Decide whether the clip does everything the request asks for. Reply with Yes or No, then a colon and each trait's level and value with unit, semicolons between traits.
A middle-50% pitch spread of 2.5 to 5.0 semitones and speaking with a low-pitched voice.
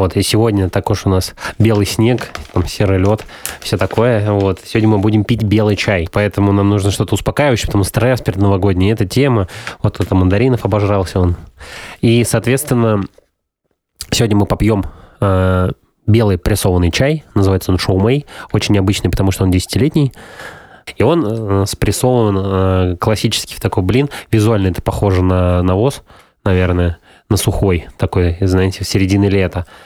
Yes: average, 3.1 semitones; low, 100 Hz